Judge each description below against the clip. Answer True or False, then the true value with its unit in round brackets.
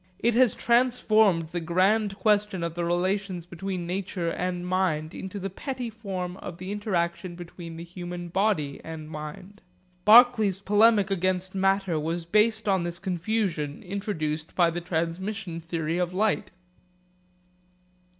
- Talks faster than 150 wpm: False (140 wpm)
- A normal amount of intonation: True (3.3 semitones)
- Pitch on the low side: False (185 Hz)